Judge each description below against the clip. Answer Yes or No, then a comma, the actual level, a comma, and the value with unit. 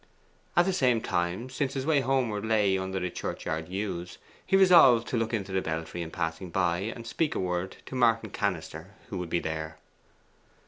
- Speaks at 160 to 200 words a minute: Yes, average, 190 wpm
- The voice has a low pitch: Yes, low, 100 Hz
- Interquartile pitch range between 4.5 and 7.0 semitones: Yes, wide, 5.6 semitones